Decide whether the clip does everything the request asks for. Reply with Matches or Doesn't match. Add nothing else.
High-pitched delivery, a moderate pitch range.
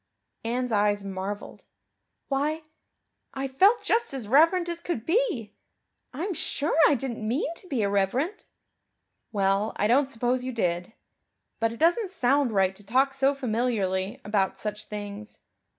Doesn't match